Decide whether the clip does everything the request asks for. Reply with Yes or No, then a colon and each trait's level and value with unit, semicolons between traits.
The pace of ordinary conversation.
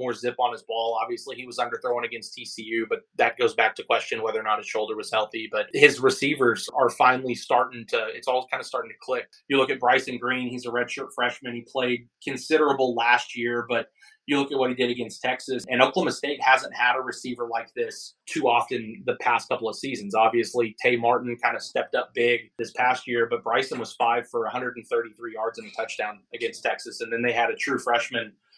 No: fast, 225 wpm